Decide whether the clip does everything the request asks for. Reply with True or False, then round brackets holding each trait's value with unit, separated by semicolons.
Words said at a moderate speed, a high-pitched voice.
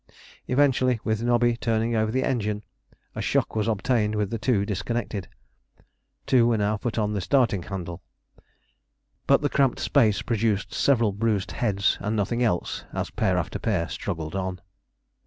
False (160 wpm; 110 Hz)